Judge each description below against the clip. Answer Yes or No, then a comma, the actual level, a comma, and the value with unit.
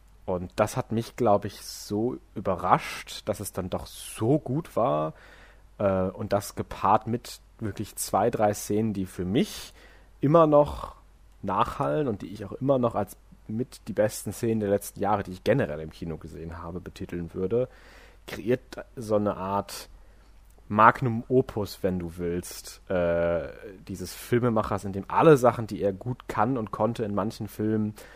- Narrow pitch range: No, average, 3.5 semitones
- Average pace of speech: Yes, average, 165 wpm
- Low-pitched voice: Yes, low, 105 Hz